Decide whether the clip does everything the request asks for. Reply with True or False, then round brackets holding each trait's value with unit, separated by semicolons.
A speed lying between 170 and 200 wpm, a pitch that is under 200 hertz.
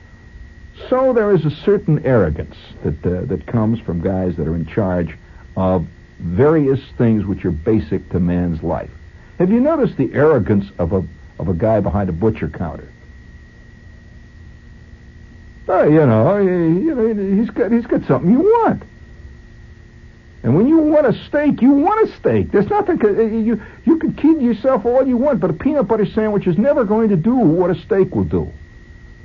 True (175 wpm; 135 Hz)